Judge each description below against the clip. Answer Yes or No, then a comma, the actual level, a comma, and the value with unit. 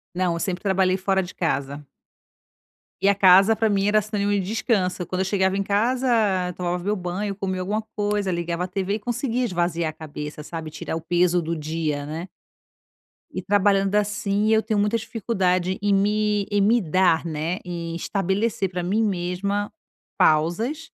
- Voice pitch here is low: No, high, 190 Hz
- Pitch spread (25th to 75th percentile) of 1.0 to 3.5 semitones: Yes, average, 2.9 semitones